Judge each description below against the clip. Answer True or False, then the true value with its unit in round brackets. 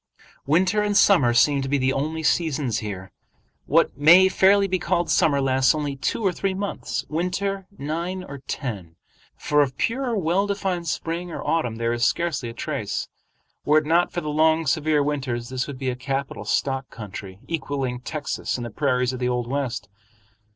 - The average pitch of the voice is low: False (145 Hz)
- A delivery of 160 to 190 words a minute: True (185 wpm)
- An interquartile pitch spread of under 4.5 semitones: False (5.2 semitones)